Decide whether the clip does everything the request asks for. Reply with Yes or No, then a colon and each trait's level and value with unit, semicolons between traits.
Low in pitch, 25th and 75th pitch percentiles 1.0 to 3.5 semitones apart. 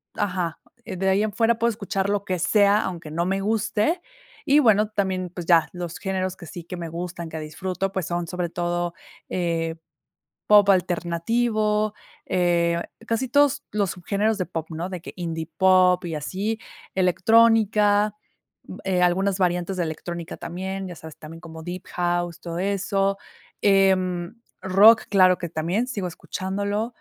No: medium, 185 Hz; average, 2.9 semitones